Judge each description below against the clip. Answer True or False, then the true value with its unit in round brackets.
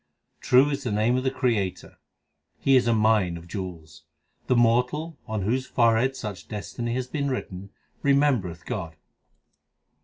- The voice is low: True (115 Hz)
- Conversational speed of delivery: True (150 wpm)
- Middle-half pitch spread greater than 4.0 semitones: True (4.8 semitones)